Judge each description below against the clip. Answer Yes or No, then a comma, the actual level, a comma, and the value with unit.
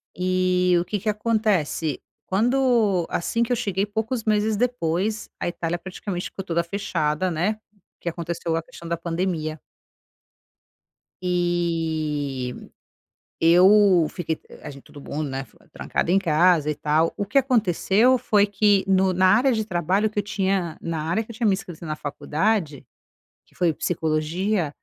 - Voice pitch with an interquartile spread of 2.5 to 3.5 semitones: No, average, 4.3 semitones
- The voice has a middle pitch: Yes, medium, 180 Hz